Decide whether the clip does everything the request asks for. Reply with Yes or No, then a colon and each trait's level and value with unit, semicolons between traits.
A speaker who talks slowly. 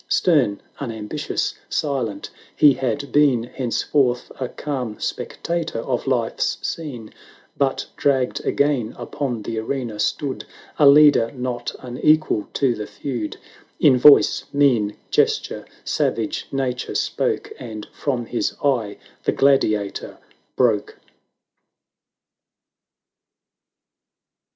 Yes: slow, 110 wpm